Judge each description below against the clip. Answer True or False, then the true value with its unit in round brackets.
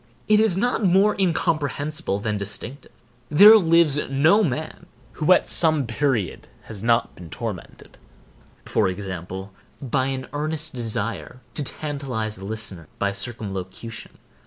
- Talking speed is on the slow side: True (130 wpm)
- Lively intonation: True (7.2 semitones)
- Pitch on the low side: True (130 Hz)